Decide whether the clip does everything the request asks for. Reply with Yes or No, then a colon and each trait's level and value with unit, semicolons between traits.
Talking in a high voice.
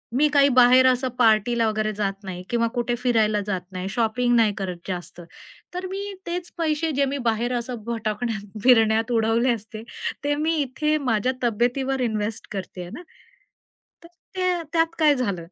Yes: high, 235 Hz